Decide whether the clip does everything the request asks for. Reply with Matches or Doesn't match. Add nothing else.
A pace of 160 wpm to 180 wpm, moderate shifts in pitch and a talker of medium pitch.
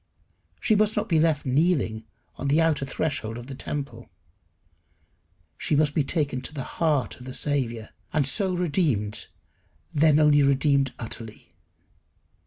Doesn't match